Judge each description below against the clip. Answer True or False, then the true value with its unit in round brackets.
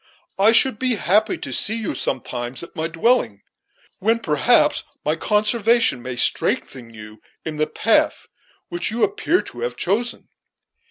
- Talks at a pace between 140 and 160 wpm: True (150 wpm)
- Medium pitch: True (180 Hz)